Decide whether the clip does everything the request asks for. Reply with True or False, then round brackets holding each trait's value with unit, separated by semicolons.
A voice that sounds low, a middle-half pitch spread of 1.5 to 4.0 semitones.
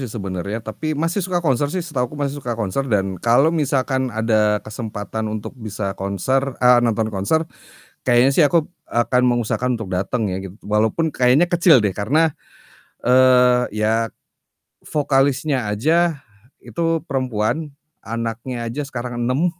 False (125 Hz; 4.7 semitones)